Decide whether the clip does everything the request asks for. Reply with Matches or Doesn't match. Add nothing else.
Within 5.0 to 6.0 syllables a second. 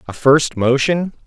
Doesn't match